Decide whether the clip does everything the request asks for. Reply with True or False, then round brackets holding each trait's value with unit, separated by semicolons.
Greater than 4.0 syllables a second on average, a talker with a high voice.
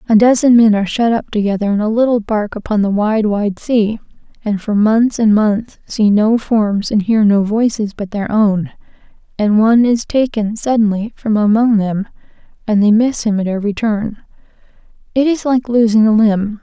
True (4.9 syllables/s; 215 Hz)